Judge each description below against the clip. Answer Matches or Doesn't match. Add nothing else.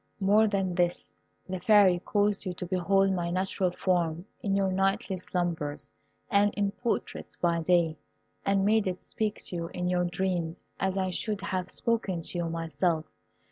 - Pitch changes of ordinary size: Doesn't match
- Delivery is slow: Doesn't match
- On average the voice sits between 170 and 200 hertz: Matches